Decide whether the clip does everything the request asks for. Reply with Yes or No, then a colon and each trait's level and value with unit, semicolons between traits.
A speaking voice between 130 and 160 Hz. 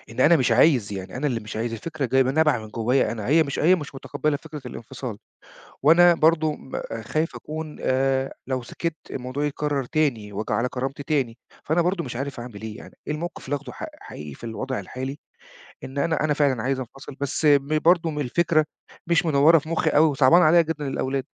Yes: medium, 140 Hz